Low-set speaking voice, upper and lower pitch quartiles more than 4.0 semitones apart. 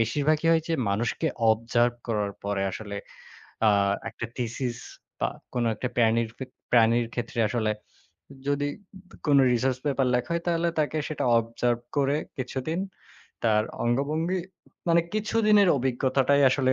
Yes: low, 130 Hz; average, 4.4 semitones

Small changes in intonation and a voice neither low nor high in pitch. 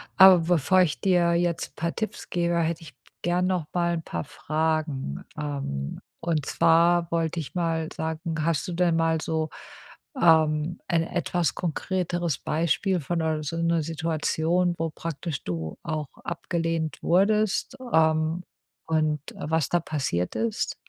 Yes: narrow, 1.8 semitones; medium, 165 Hz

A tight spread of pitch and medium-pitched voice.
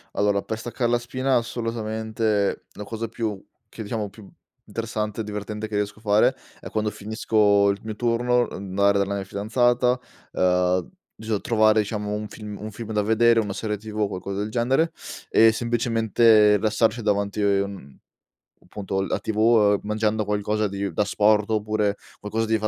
No: narrow, 1.7 semitones; low, 105 Hz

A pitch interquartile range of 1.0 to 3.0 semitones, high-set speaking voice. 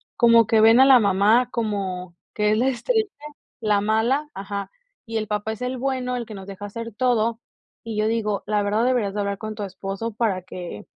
Yes: average, 2.7 semitones; high, 220 Hz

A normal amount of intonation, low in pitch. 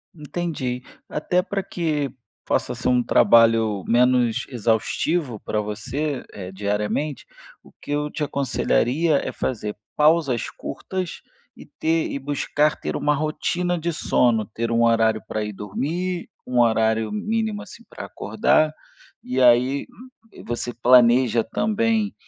No: wide, 5.8 semitones; low, 130 Hz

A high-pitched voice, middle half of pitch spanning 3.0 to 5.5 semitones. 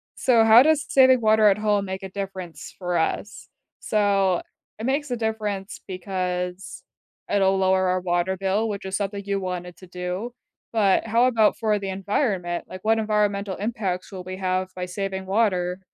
No: high, 195 Hz; narrow, 2.6 semitones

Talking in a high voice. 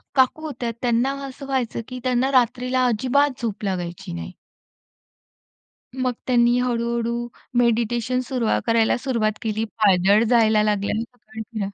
Yes: high, 235 Hz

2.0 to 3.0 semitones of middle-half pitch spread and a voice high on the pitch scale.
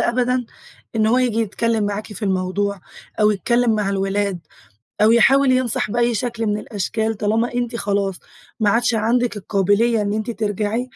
Yes: narrow, 2.6 semitones; high, 220 Hz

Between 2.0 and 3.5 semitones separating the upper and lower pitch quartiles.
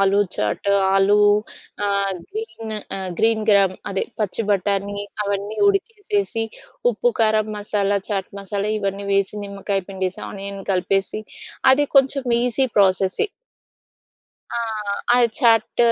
Yes: narrow, 2.4 semitones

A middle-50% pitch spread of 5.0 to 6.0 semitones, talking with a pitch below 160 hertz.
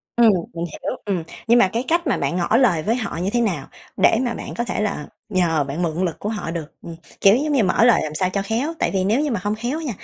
No: wide, 5.6 semitones; high, 210 Hz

